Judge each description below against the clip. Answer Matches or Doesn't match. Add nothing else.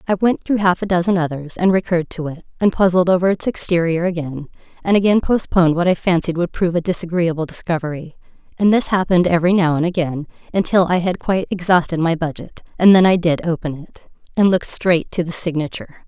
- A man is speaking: Doesn't match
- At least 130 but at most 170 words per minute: Doesn't match